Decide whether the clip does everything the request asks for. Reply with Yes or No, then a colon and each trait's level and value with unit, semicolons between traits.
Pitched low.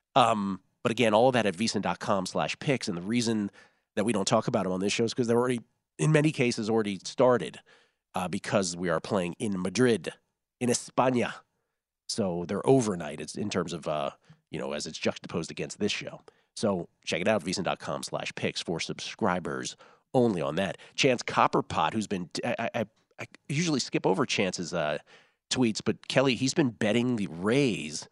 Yes: low, 115 Hz